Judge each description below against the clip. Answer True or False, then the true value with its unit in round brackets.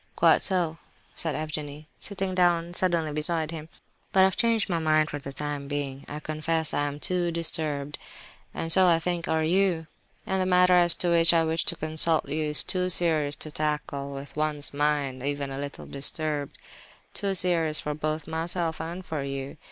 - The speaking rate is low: False (190 wpm)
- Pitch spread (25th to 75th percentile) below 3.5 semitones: True (2.8 semitones)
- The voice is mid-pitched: True (155 Hz)